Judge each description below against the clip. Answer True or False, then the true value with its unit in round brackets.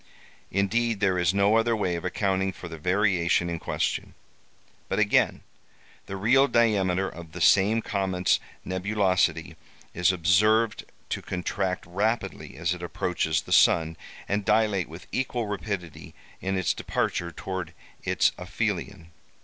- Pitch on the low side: True (95 Hz)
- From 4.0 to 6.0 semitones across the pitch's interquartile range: False (2.9 semitones)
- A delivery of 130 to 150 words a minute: True (135 wpm)